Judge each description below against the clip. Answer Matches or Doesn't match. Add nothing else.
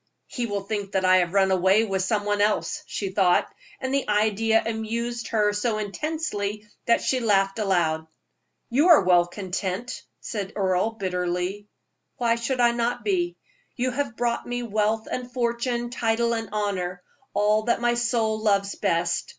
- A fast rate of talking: Doesn't match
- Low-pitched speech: Doesn't match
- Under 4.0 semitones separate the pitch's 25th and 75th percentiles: Matches